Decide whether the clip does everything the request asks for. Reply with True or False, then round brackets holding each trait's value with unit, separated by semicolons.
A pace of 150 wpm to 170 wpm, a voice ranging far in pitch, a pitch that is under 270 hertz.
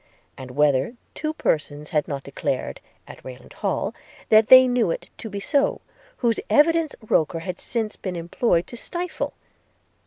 True (155 wpm; 9.0 semitones; 190 Hz)